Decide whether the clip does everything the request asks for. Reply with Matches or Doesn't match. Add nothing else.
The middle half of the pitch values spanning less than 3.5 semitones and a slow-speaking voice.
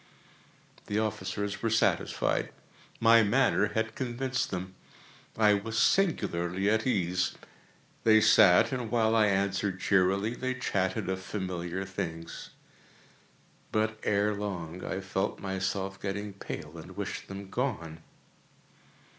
Matches